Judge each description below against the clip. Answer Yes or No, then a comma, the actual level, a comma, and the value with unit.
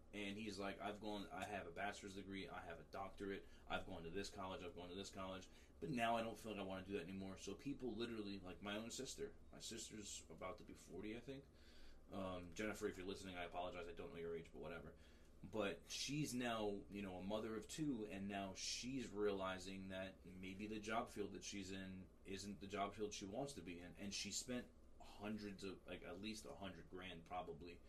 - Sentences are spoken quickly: Yes, fast, 230 wpm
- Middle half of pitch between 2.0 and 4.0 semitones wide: Yes, average, 2.9 semitones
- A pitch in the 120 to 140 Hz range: No, low, 100 Hz